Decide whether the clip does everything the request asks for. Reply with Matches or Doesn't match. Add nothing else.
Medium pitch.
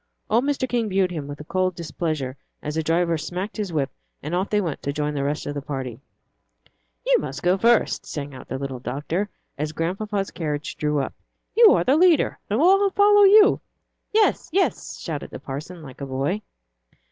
Matches